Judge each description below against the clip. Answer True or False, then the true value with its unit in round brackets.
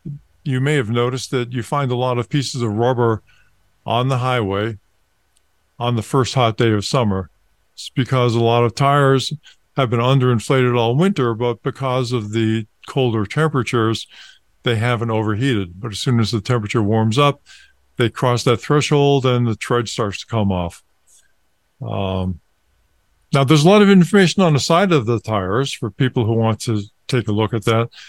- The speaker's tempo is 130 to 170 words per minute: False (180 wpm)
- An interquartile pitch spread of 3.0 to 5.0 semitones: True (3.4 semitones)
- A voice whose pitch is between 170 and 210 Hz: False (120 Hz)